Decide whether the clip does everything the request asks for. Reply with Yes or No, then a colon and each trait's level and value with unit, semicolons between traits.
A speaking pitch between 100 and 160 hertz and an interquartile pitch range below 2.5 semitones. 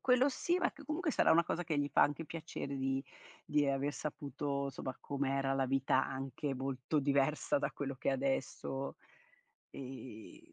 Yes: medium, 140 Hz; narrow, 2.1 semitones